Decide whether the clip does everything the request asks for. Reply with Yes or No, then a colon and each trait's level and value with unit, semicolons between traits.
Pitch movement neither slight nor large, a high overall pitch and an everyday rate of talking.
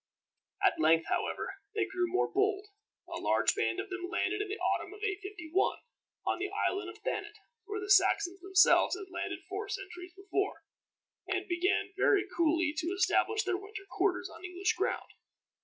No: narrow, 2.1 semitones; very high, 385 Hz; average, 170 wpm